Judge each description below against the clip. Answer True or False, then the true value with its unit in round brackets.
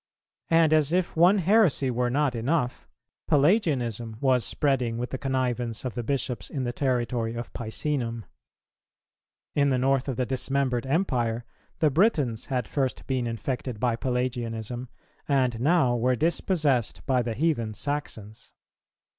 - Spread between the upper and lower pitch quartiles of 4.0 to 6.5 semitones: False (3.4 semitones)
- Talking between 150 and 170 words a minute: False (140 wpm)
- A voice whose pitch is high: False (130 Hz)